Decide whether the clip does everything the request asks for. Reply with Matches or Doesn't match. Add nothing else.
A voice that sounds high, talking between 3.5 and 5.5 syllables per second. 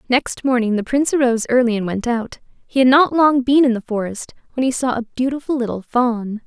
Doesn't match